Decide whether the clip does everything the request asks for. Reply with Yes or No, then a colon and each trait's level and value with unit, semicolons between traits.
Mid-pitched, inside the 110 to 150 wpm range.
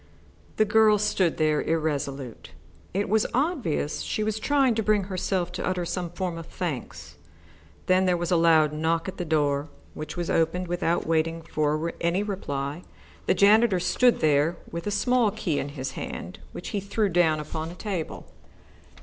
No: medium, 175 Hz; average, 175 wpm